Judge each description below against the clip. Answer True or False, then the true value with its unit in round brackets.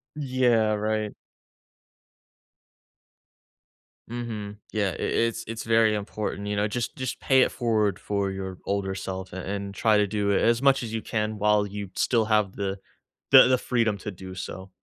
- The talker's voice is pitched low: True (105 Hz)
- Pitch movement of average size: False (2.3 semitones)